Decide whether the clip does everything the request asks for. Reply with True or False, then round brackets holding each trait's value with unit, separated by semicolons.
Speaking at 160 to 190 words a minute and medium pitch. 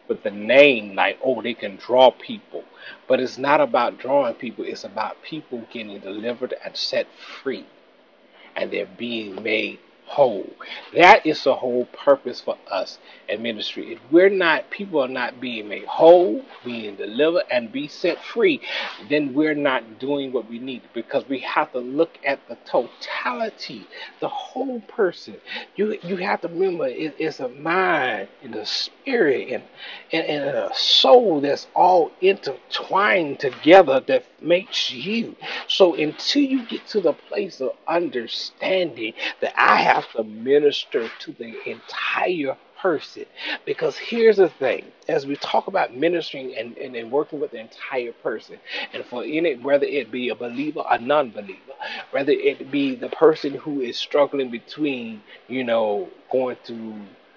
True (165 wpm; 155 Hz)